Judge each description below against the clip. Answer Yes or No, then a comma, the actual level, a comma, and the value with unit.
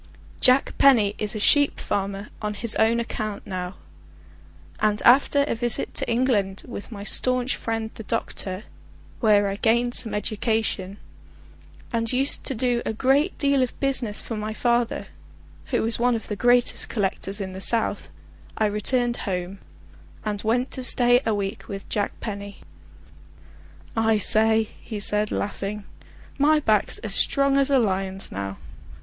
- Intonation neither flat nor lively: Yes, average, 3.2 semitones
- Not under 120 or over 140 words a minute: No, average, 155 wpm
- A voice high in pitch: Yes, high, 220 Hz